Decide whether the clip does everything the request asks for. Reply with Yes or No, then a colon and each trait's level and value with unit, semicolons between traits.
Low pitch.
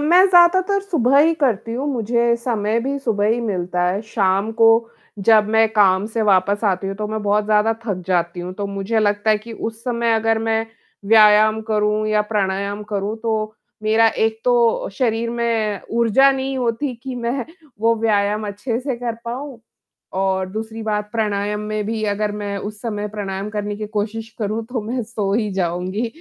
No: high, 215 Hz